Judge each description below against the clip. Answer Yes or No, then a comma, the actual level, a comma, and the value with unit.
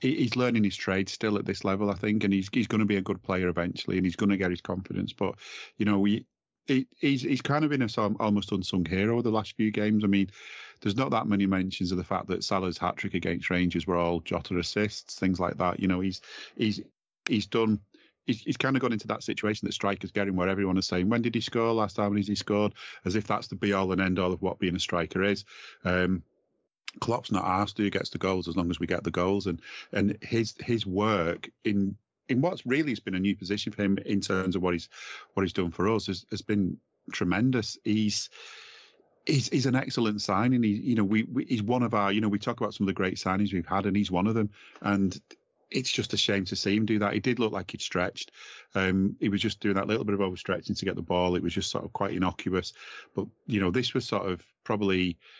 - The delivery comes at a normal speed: No, fast, 255 wpm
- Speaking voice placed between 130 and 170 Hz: No, low, 100 Hz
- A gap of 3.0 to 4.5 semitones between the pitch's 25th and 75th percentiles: No, narrow, 2.5 semitones